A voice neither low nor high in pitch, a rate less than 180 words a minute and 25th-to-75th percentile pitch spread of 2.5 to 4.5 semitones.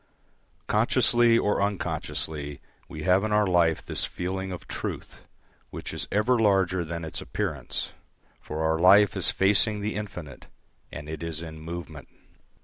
No: very low, 90 Hz; average, 145 wpm; average, 4.2 semitones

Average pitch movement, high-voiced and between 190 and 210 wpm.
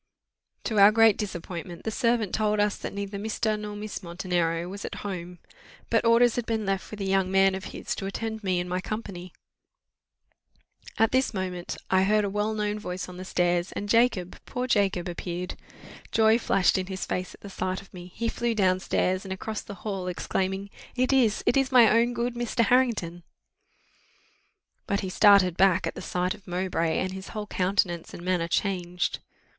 Yes: average, 3.1 semitones; high, 195 Hz; average, 195 wpm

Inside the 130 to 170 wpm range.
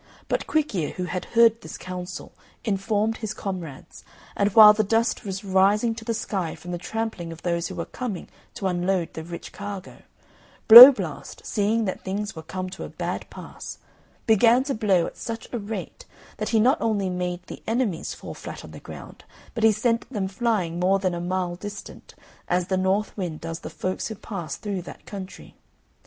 No: average, 195 wpm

